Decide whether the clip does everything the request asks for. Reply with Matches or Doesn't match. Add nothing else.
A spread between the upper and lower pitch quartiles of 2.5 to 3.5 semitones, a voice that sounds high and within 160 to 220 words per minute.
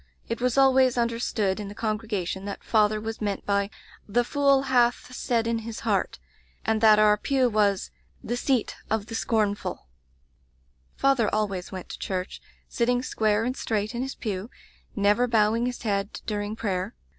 Matches